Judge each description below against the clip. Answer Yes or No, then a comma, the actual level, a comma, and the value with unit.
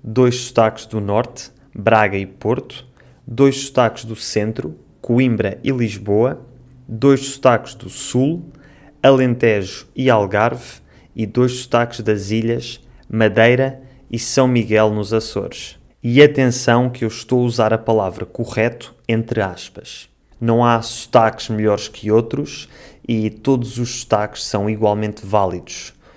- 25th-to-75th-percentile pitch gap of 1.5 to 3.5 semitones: Yes, average, 2.7 semitones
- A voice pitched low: Yes, low, 115 Hz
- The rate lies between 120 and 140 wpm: Yes, average, 130 wpm